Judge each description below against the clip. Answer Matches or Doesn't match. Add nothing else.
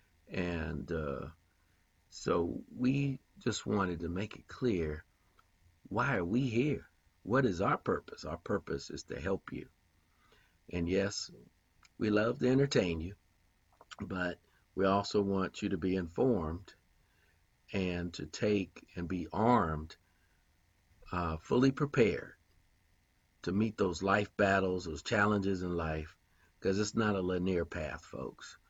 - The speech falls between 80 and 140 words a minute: Matches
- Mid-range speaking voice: Doesn't match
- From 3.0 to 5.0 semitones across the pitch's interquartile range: Matches